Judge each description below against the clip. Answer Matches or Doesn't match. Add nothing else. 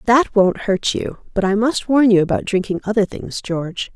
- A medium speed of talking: Doesn't match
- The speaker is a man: Doesn't match